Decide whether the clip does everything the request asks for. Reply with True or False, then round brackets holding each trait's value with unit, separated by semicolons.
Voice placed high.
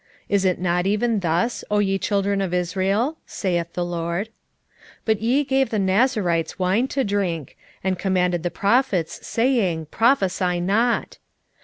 True (195 Hz)